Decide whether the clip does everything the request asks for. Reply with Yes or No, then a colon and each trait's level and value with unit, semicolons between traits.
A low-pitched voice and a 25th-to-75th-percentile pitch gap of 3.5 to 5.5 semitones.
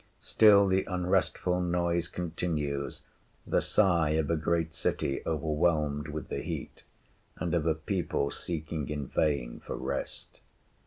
No: very low, 80 Hz; average, 2.7 semitones